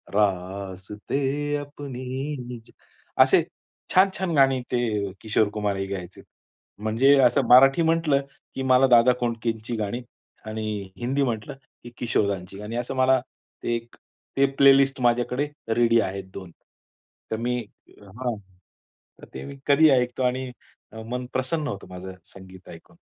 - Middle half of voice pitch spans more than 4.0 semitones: Yes, average, 4.5 semitones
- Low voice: Yes, low, 120 Hz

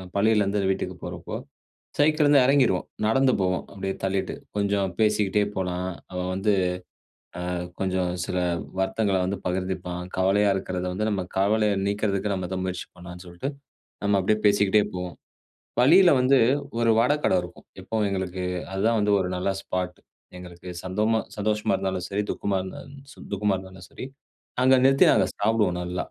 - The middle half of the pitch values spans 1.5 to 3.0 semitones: Yes, narrow, 2.5 semitones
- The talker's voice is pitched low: Yes, low, 100 Hz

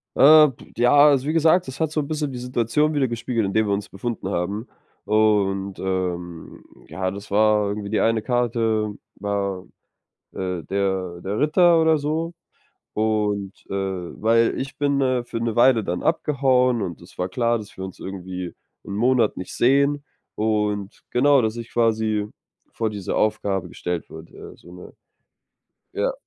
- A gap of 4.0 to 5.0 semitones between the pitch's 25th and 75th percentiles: Yes, average, 4.7 semitones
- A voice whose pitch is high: No, low, 110 Hz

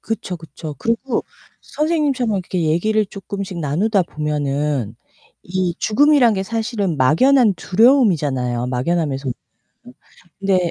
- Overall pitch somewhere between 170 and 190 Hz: Yes, medium, 185 Hz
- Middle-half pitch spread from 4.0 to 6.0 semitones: No, wide, 6.9 semitones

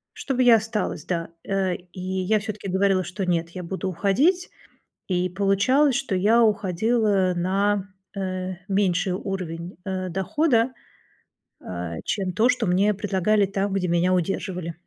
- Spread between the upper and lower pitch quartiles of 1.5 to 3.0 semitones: Yes, narrow, 2.5 semitones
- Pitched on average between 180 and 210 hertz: Yes, high, 190 Hz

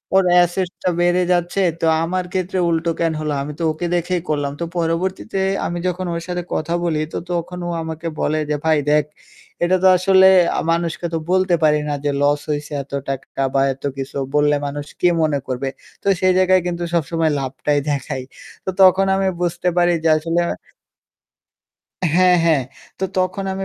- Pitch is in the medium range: Yes, medium, 170 Hz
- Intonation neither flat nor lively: Yes, average, 3.3 semitones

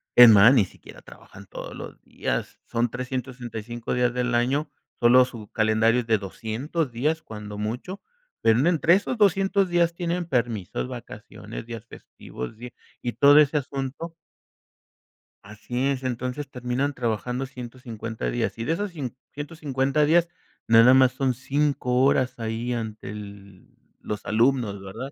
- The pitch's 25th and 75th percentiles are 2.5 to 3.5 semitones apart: No, average, 3.9 semitones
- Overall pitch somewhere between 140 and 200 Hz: No, low, 125 Hz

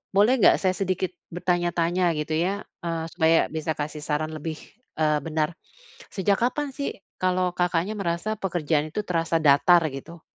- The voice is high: No, medium, 170 Hz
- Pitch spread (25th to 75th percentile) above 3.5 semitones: No, average, 2.7 semitones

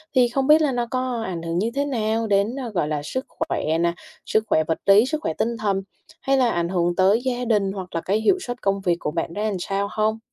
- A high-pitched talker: Yes, high, 215 Hz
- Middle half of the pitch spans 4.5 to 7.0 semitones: Yes, wide, 5.4 semitones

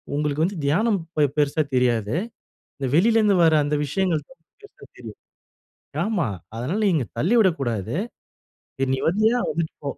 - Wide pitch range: Yes, wide, 6.2 semitones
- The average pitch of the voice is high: No, medium, 155 Hz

